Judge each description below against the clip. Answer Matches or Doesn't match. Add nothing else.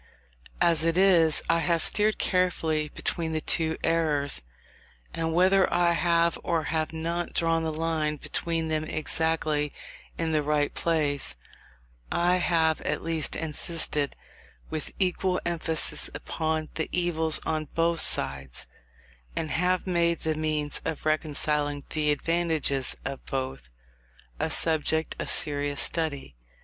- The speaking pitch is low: Doesn't match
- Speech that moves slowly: Matches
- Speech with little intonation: Matches